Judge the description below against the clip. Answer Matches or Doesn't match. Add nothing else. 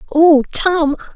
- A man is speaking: Doesn't match